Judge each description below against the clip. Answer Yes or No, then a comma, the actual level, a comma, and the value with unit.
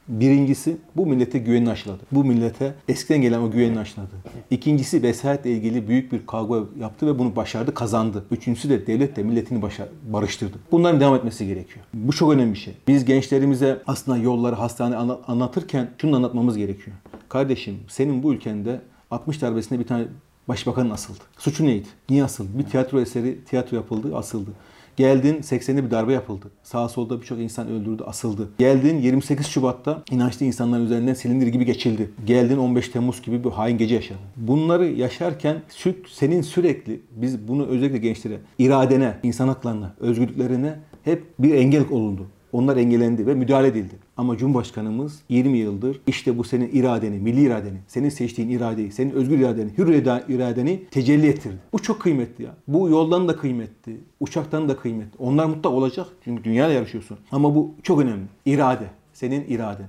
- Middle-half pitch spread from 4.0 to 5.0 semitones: No, average, 3.3 semitones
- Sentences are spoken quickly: Yes, fast, 165 wpm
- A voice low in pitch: Yes, low, 125 Hz